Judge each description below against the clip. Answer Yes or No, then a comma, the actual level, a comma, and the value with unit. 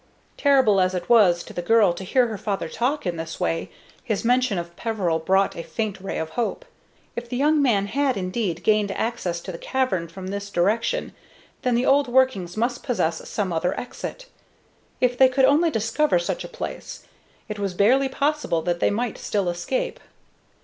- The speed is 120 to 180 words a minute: No, average, 190 wpm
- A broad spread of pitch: Yes, wide, 5.9 semitones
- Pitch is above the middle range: Yes, high, 215 Hz